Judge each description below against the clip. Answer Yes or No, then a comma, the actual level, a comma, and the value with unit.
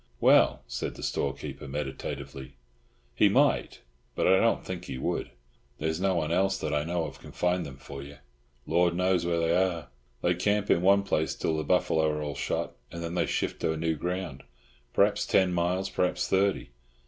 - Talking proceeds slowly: No, average, 190 wpm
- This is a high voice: No, very low, 85 Hz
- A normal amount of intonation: Yes, average, 3.2 semitones